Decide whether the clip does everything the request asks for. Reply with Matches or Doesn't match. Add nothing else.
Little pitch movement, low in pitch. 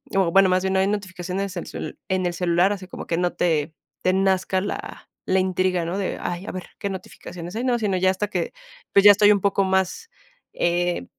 Doesn't match